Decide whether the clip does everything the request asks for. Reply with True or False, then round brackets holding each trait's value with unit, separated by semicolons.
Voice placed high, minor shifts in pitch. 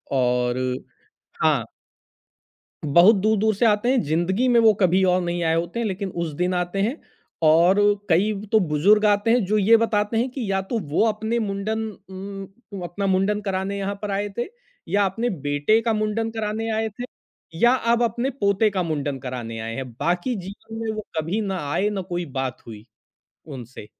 False (200 Hz; 4.1 semitones)